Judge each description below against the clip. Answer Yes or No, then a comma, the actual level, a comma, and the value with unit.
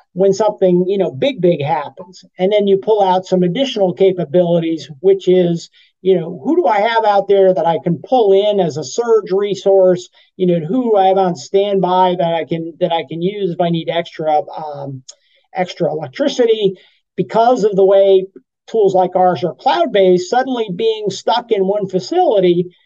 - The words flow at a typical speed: Yes, average, 185 wpm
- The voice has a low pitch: No, high, 190 Hz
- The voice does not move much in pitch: Yes, narrow, 2.3 semitones